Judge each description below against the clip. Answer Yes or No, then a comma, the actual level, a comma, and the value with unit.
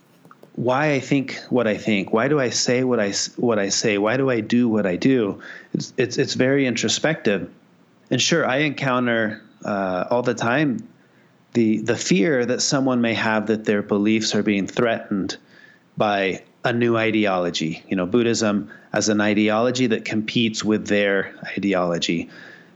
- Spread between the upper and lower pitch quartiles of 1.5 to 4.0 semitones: Yes, average, 3.0 semitones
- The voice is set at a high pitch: No, low, 110 Hz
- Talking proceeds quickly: No, average, 165 wpm